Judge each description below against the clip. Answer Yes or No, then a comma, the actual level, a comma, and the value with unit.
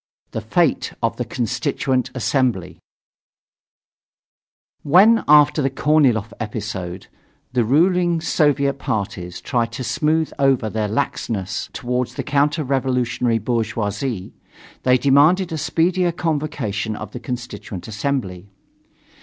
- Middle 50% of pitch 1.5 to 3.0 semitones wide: No, average, 5.1 semitones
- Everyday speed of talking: No, slow, 110 wpm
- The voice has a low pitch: Yes, low, 125 Hz